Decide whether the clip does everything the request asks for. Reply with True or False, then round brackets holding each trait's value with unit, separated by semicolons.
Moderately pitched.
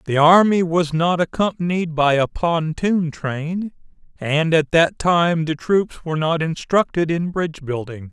True (165 Hz)